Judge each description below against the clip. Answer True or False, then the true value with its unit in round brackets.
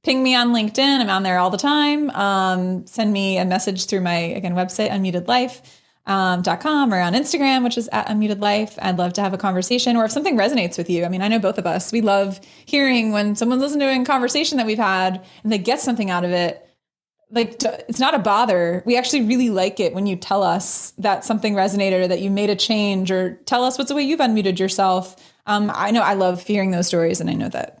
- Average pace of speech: False (240 wpm)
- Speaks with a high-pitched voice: True (205 Hz)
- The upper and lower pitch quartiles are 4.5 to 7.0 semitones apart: True (4.8 semitones)